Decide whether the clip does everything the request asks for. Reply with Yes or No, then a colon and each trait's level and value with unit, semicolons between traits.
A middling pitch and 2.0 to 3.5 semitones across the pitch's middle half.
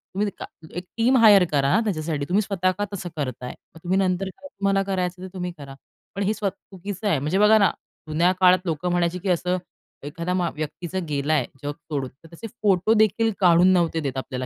No: medium, 180 Hz; average, 3.9 semitones